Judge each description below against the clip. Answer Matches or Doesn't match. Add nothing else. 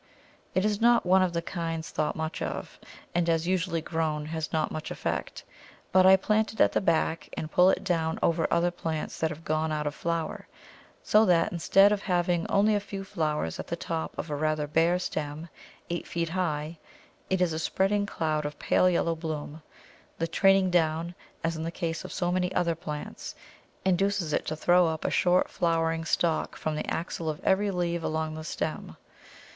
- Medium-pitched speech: Matches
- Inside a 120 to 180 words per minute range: Doesn't match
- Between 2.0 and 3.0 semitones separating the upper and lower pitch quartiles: Matches